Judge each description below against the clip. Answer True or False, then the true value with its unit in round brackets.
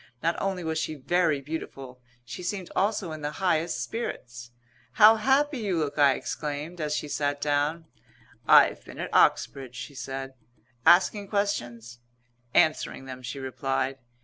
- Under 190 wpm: True (150 wpm)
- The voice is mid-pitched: True (150 Hz)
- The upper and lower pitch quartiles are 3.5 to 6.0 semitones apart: True (5.1 semitones)